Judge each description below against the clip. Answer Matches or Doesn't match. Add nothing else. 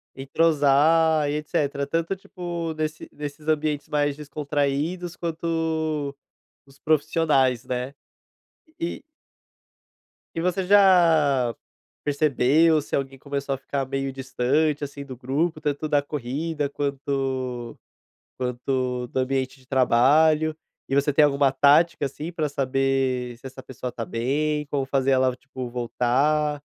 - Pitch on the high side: Doesn't match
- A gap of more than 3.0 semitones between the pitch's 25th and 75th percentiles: Doesn't match